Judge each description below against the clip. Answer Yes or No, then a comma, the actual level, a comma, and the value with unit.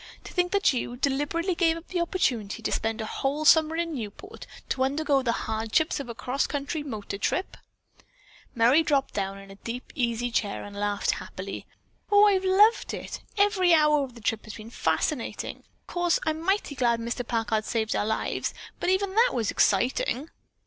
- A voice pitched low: No, very high, 270 Hz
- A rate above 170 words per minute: Yes, average, 185 wpm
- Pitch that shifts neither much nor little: No, wide, 6.8 semitones